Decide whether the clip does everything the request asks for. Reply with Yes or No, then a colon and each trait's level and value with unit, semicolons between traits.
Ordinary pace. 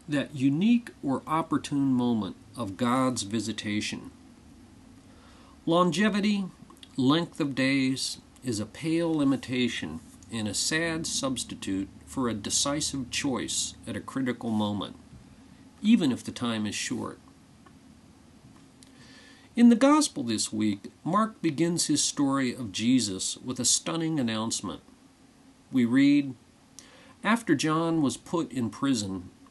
No: slow, 115 wpm